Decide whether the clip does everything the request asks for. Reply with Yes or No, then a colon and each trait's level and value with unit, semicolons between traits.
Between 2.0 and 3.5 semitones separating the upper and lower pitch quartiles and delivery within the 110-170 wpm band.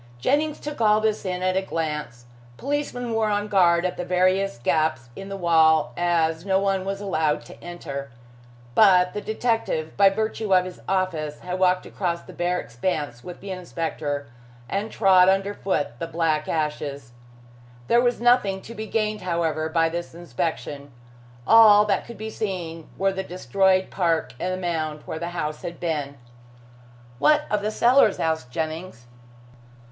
No: average, 4.0 semitones; average, 165 wpm